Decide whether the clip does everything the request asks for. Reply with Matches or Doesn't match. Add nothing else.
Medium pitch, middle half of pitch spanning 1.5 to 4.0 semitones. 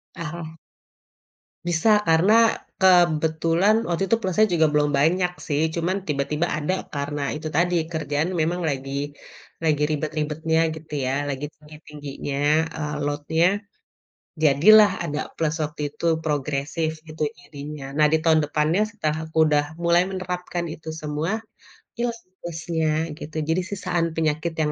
Matches